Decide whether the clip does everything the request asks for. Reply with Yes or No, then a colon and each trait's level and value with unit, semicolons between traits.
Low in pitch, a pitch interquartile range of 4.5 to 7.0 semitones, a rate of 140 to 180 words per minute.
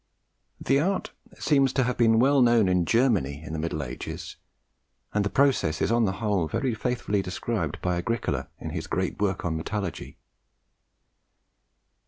Yes: low, 105 Hz; wide, 5.6 semitones; average, 160 wpm